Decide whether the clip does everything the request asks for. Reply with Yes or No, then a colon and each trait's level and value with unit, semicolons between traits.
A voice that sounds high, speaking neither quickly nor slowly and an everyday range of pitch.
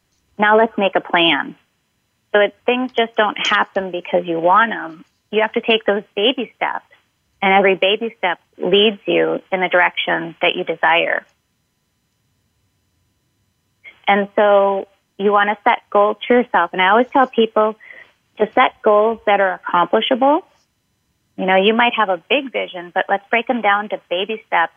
Yes: high, 200 Hz; average, 170 wpm; average, 4.0 semitones